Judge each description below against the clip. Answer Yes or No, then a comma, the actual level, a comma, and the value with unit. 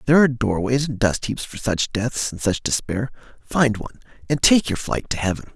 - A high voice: No, low, 115 Hz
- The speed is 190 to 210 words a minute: Yes, fast, 205 wpm